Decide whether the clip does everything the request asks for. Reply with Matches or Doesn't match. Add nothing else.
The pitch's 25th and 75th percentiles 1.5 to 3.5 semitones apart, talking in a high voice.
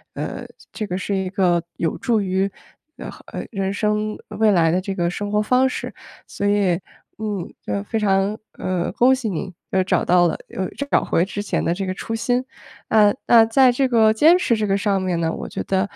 Matches